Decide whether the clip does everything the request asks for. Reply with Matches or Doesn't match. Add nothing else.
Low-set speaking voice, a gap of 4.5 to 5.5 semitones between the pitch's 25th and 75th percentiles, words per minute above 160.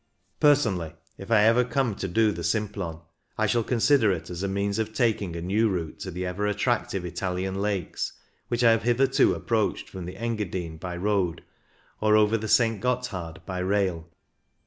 Doesn't match